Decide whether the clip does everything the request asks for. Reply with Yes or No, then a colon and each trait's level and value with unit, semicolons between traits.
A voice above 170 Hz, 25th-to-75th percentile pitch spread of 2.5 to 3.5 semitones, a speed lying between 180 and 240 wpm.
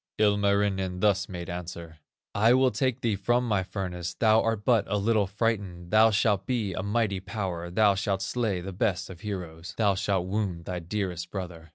No: low, 100 Hz; average, 3.2 semitones; average, 185 wpm